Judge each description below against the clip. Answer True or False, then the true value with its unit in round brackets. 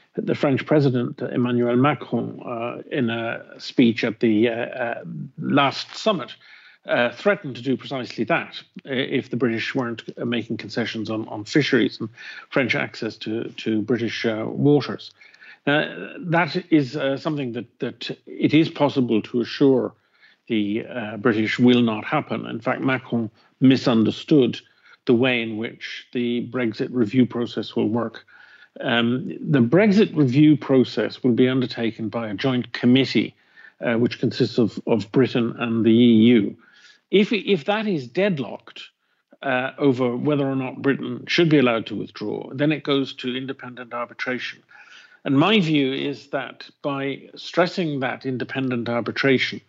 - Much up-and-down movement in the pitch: False (3.1 semitones)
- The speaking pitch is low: True (125 Hz)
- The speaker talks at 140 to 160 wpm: True (150 wpm)